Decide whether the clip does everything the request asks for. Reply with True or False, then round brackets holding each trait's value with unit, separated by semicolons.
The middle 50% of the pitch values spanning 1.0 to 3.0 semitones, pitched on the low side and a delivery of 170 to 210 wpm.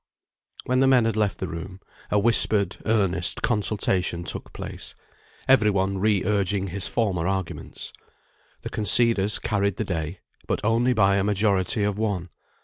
False (2.5 semitones; 100 Hz; 150 wpm)